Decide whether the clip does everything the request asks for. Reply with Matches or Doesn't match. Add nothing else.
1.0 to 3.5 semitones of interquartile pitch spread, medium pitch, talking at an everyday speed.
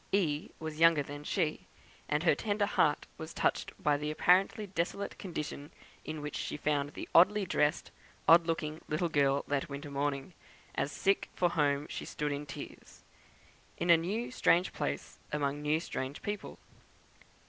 Matches